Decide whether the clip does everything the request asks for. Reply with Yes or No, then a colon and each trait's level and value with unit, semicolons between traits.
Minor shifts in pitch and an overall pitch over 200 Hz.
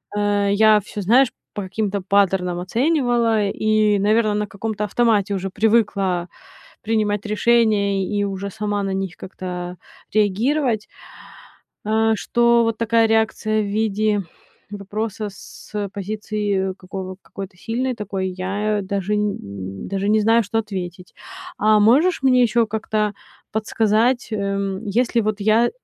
Yes: narrow, 2.1 semitones; high, 210 Hz